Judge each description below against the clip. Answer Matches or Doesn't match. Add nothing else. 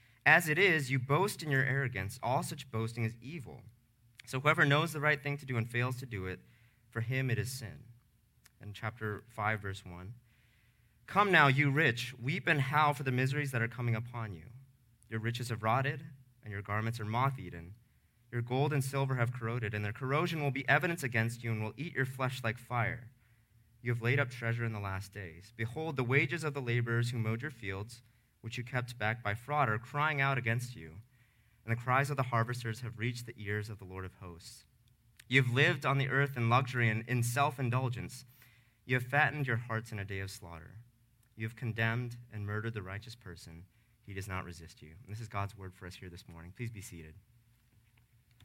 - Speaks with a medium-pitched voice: Doesn't match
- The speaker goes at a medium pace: Doesn't match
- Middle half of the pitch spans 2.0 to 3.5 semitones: Matches